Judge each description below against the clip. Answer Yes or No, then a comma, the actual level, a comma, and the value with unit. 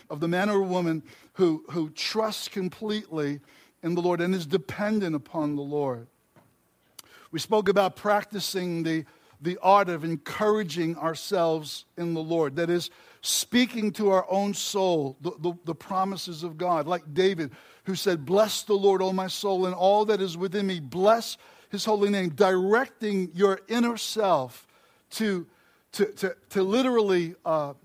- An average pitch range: Yes, average, 3.4 semitones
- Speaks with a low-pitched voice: No, medium, 185 Hz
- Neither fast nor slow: Yes, average, 160 wpm